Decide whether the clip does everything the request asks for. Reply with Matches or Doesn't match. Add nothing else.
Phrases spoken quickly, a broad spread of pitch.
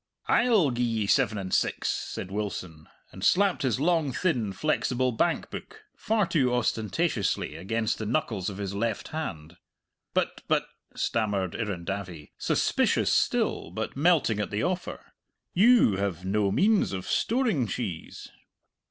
Doesn't match